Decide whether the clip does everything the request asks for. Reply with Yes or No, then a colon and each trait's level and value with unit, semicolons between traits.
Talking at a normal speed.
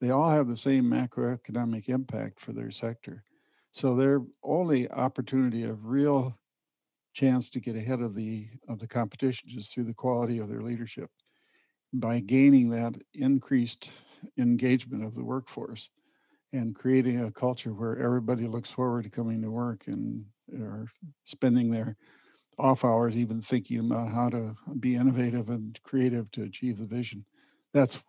Yes: average, 155 wpm